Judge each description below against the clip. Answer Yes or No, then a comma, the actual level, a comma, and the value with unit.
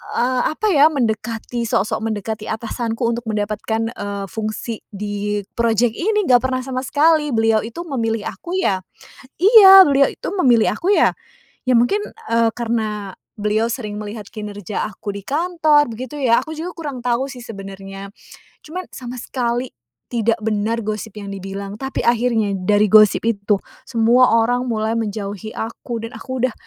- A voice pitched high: Yes, high, 230 Hz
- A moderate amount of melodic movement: Yes, average, 3.4 semitones